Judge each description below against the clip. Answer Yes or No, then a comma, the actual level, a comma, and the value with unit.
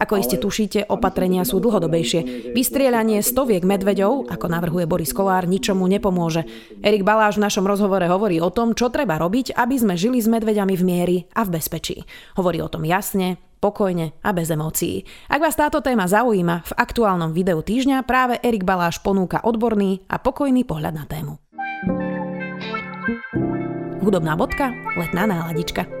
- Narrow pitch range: No, average, 4.4 semitones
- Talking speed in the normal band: Yes, average, 155 wpm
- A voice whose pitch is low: No, high, 195 Hz